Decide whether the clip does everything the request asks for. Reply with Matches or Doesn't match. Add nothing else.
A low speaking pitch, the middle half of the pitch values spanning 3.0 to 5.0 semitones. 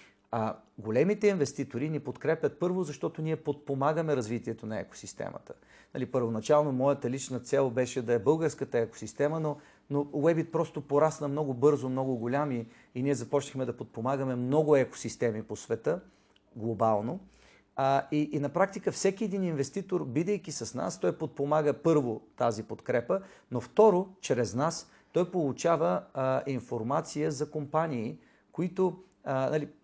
Doesn't match